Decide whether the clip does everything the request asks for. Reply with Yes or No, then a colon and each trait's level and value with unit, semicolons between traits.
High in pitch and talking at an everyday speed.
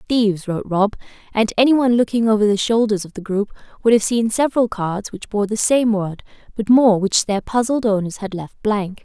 No: high, 215 Hz; fast, 210 wpm